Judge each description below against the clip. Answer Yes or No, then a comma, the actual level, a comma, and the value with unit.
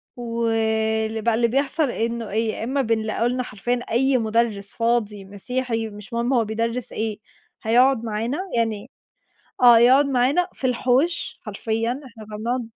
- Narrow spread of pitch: Yes, narrow, 2.2 semitones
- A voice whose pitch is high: Yes, high, 230 Hz